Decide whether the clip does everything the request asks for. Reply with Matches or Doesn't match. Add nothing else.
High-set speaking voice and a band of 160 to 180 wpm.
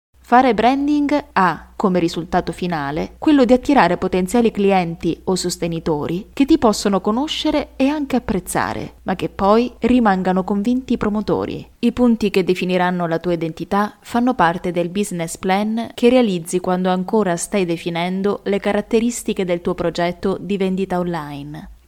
Doesn't match